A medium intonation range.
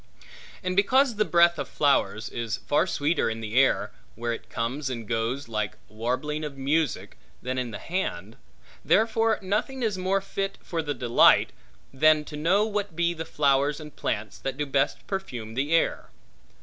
No: wide, 7.0 semitones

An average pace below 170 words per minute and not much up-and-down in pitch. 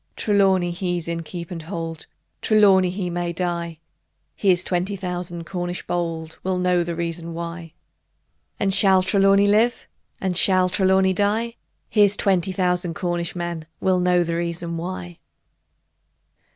Yes: average, 140 wpm; narrow, 1.9 semitones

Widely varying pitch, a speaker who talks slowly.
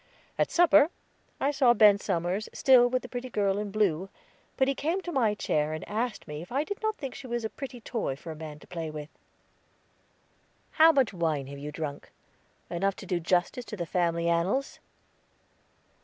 No: wide, 7.4 semitones; average, 195 wpm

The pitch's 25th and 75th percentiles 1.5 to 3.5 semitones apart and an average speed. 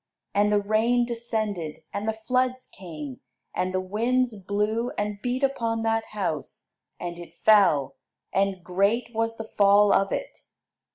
Yes: average, 3.0 semitones; average, 150 wpm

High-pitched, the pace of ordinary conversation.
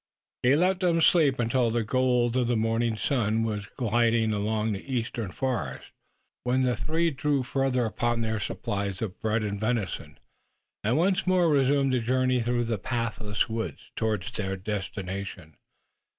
No: low, 115 Hz; average, 150 wpm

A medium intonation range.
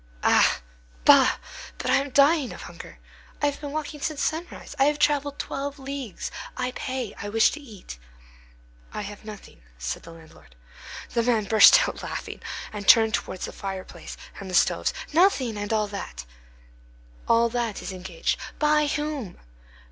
No: wide, 6.1 semitones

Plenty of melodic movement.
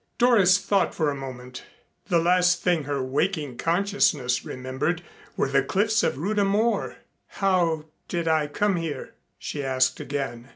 Yes: wide, 6.0 semitones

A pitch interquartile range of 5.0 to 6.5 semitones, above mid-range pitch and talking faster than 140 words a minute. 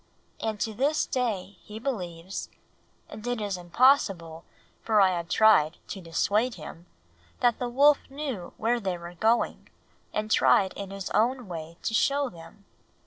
Yes: wide, 5.5 semitones; high, 210 Hz; average, 155 wpm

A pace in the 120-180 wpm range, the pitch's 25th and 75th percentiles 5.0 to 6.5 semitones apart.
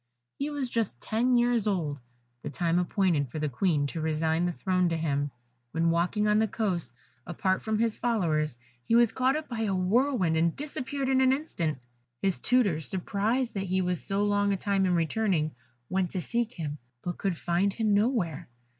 No: average, 190 wpm; wide, 5.4 semitones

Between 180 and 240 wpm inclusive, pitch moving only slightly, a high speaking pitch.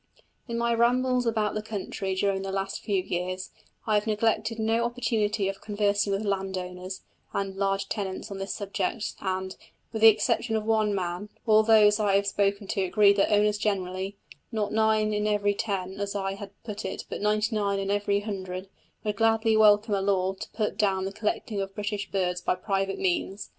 Yes: average, 190 wpm; narrow, 1.9 semitones; high, 205 Hz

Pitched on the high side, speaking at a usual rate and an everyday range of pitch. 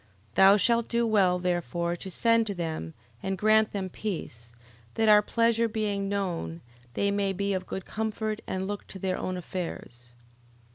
Yes: high, 195 Hz; average, 175 wpm; average, 3.3 semitones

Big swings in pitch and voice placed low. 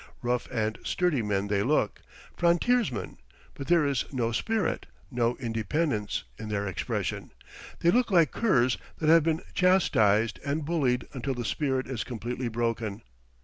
Yes: wide, 6.2 semitones; low, 125 Hz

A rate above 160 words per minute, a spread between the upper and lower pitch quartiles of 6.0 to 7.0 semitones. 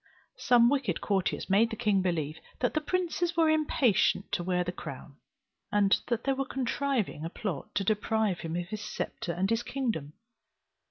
Yes: average, 175 wpm; wide, 6.4 semitones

